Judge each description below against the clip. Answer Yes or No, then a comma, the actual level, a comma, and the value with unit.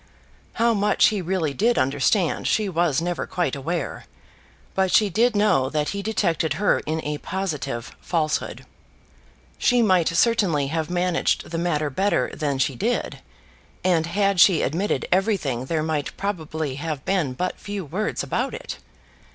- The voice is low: No, medium, 175 Hz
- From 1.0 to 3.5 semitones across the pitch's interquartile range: No, average, 4.7 semitones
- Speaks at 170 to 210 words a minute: No, average, 150 wpm